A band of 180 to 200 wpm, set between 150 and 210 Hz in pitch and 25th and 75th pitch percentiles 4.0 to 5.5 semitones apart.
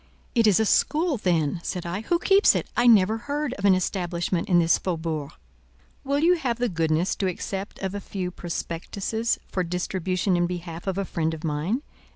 Yes: average, 195 wpm; medium, 185 Hz; average, 4.6 semitones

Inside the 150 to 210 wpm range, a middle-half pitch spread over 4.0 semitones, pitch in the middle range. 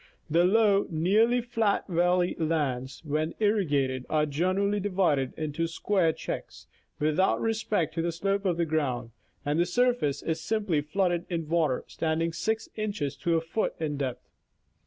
Yes: average, 155 wpm; average, 4.7 semitones; medium, 170 Hz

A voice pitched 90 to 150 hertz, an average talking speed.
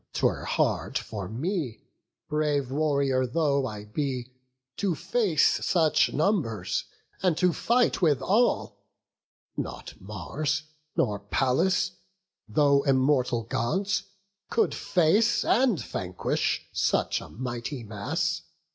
No: medium, 140 Hz; slow, 105 wpm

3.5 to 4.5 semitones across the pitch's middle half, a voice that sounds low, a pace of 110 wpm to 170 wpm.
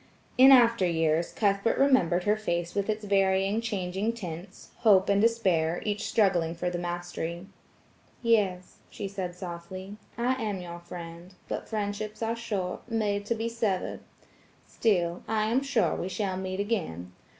No: average, 3.9 semitones; high, 195 Hz; average, 140 wpm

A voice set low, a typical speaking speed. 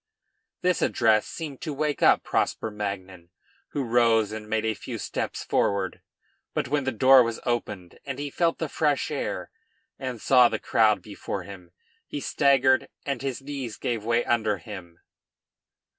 Yes: low, 120 Hz; average, 160 wpm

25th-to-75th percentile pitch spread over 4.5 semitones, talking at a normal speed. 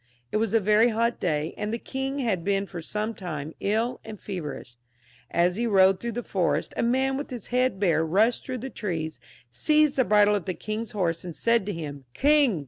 No: average, 5.0 semitones; fast, 215 wpm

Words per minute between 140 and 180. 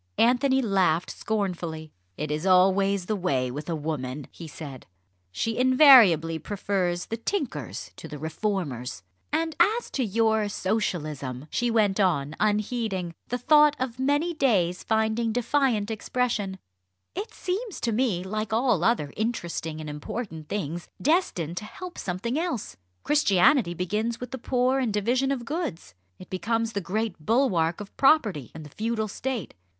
Yes: average, 150 wpm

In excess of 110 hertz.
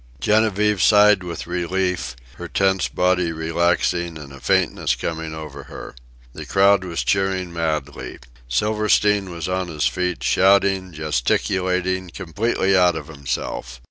No: very low, 90 Hz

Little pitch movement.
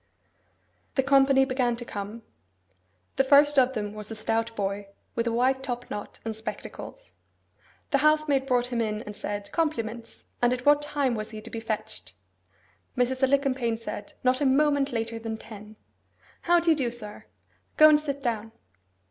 No: average, 3.7 semitones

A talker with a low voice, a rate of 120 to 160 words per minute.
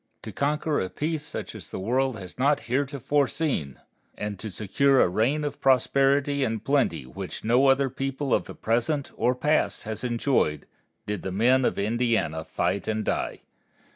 No: low, 125 Hz; average, 175 wpm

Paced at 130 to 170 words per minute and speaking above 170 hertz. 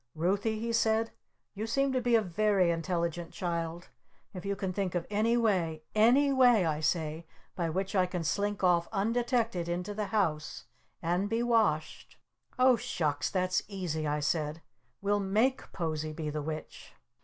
Yes: average, 165 wpm; medium, 185 Hz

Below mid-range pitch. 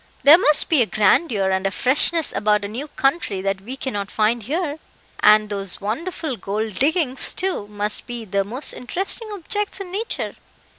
No: high, 240 Hz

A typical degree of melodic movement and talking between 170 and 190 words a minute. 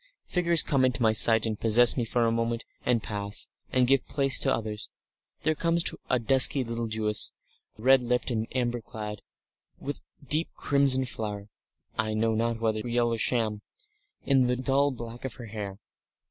Yes: average, 3.1 semitones; average, 175 wpm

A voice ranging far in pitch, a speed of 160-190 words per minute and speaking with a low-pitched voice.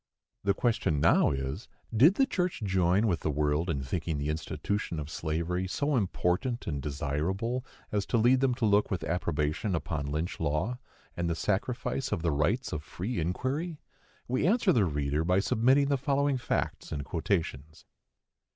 Yes: wide, 7.9 semitones; average, 170 wpm; very low, 90 Hz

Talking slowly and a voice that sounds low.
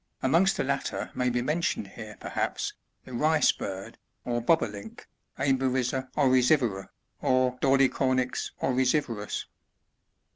Yes: slow, 120 wpm; low, 130 Hz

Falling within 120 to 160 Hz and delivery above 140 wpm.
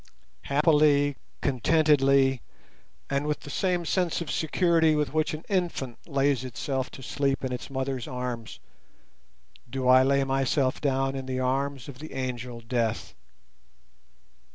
No: low, 135 Hz; slow, 135 wpm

